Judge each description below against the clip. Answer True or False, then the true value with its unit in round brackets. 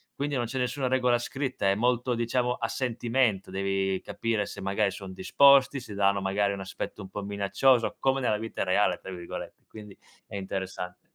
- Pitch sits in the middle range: False (105 Hz)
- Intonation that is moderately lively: True (4.3 semitones)